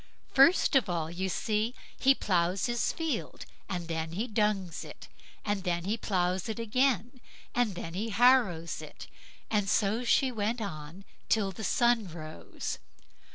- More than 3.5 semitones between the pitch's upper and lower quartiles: Yes, average, 5.1 semitones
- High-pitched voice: Yes, high, 205 Hz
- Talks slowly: No, average, 155 wpm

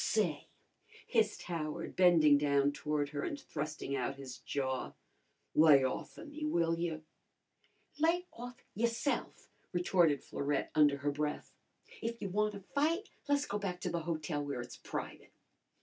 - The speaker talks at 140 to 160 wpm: Yes, average, 150 wpm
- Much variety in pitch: Yes, wide, 6.6 semitones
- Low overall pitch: No, medium, 165 Hz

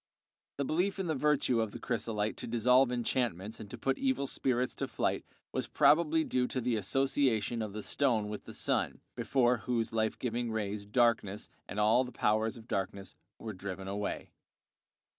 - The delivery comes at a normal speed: Yes, average, 180 wpm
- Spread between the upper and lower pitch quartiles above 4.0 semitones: No, average, 3.4 semitones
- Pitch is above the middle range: No, low, 115 Hz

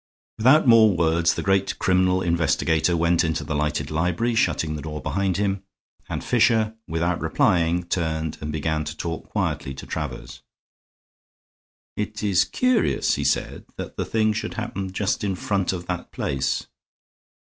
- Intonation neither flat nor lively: Yes, average, 4.3 semitones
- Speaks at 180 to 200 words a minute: No, average, 155 wpm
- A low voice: Yes, very low, 90 Hz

